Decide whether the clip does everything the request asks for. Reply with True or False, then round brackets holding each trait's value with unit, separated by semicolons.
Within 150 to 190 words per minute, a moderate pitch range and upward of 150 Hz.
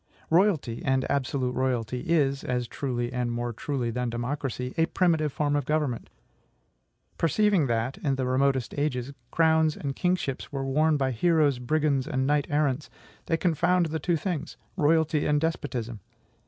False (155 wpm; 3.8 semitones; 140 Hz)